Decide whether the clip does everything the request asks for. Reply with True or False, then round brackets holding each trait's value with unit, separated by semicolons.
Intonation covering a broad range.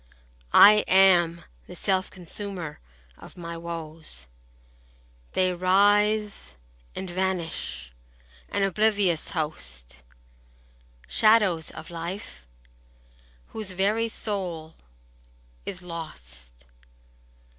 False (3.5 semitones)